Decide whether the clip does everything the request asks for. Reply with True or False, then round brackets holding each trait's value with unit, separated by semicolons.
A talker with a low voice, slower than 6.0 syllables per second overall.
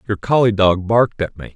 True (105 Hz; 5.8 syllables/s)